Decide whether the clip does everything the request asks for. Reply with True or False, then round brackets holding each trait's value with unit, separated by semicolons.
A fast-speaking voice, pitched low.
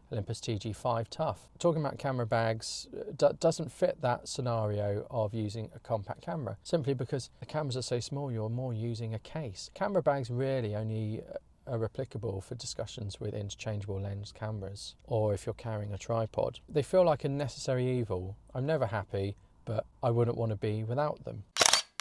False (175 wpm; 115 Hz)